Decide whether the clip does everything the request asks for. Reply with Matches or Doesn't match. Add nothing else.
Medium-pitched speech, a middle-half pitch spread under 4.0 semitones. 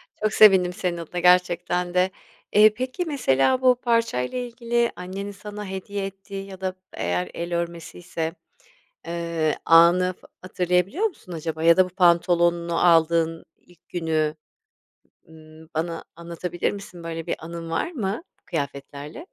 Matches